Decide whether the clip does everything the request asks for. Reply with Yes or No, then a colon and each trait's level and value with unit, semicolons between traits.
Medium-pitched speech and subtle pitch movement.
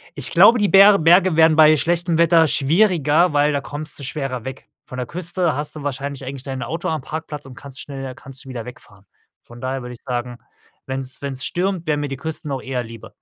No: medium, 145 Hz; average, 3.5 semitones